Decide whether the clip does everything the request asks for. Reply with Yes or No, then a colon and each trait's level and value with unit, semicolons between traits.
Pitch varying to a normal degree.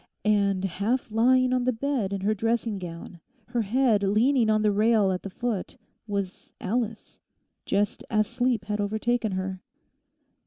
Yes: average, 3.2 semitones